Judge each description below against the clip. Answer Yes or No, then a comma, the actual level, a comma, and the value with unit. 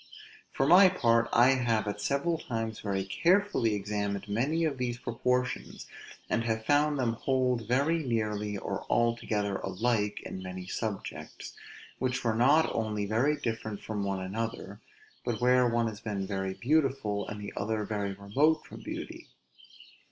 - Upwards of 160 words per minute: No, average, 150 wpm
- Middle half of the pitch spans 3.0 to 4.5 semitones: Yes, average, 3.8 semitones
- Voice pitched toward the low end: Yes, low, 115 Hz